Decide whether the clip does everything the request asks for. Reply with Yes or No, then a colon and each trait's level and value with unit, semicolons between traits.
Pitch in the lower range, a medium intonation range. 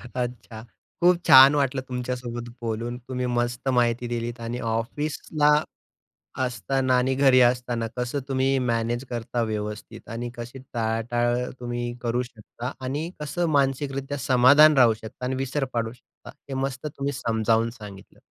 No: low, 125 Hz; narrow, 2.2 semitones